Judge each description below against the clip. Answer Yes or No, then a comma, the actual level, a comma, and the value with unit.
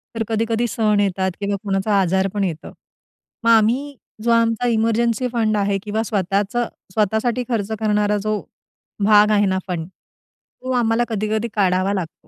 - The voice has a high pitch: Yes, high, 215 Hz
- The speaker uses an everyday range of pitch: No, narrow, 2.3 semitones